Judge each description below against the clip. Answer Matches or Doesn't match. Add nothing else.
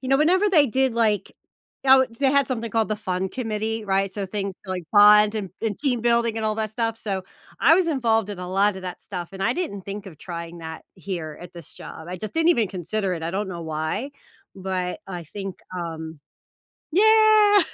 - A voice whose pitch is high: Matches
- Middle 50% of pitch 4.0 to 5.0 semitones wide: Matches